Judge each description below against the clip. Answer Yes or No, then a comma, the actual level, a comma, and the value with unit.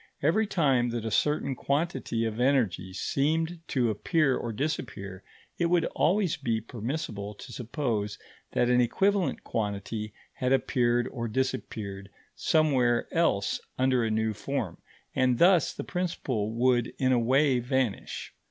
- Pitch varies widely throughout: No, average, 4.8 semitones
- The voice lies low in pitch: Yes, low, 125 Hz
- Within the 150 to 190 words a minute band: No, average, 140 wpm